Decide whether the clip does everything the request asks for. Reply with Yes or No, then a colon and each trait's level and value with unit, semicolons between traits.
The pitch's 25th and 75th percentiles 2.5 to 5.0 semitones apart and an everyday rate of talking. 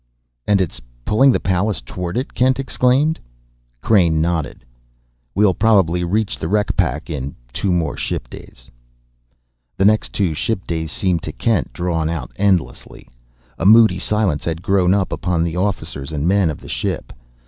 Yes: average, 4.3 semitones; average, 160 wpm